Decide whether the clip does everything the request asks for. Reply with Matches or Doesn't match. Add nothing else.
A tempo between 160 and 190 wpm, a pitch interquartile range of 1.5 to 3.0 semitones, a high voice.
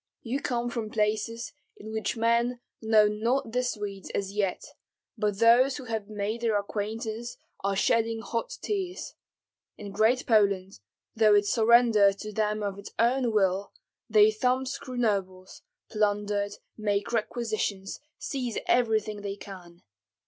Doesn't match